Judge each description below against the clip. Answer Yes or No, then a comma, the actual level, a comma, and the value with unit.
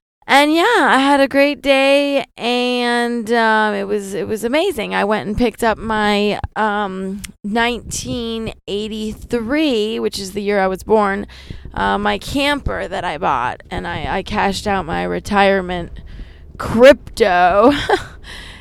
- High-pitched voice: Yes, high, 215 Hz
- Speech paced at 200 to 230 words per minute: No, average, 140 wpm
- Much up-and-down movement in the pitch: No, average, 3.7 semitones